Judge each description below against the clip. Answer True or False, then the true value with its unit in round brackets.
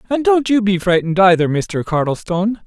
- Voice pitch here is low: False (195 Hz)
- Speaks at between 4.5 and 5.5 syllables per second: False (5.7 syllables/s)